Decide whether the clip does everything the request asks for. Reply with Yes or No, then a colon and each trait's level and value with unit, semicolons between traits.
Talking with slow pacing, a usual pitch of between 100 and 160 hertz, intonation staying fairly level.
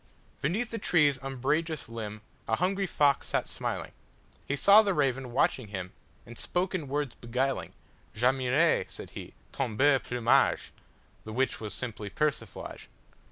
No: slow, 125 wpm; low, 135 Hz; average, 4.7 semitones